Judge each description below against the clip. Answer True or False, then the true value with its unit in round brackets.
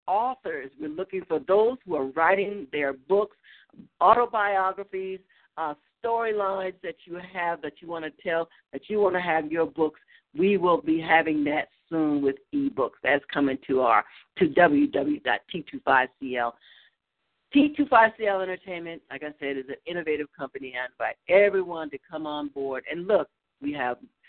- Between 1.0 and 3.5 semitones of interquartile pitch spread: False (5.1 semitones)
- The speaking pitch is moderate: True (170 Hz)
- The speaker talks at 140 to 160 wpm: True (155 wpm)